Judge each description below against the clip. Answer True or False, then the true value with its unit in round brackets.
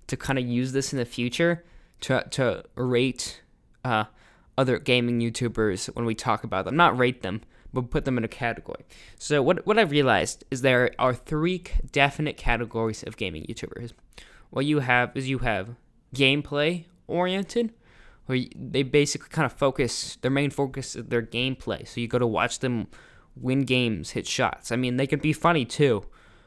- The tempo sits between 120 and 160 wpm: False (180 wpm)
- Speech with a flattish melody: False (3.1 semitones)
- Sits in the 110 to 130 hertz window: True (125 Hz)